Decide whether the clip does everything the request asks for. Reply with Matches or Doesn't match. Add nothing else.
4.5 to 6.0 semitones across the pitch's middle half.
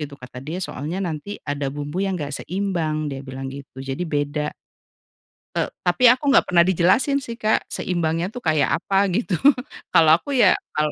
Matches